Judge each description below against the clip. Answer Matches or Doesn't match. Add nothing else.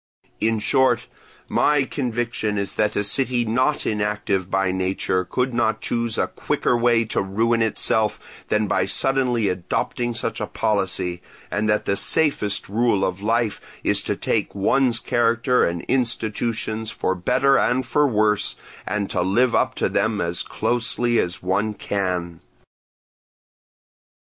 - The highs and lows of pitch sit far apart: Doesn't match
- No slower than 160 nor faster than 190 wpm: Doesn't match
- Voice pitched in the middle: Doesn't match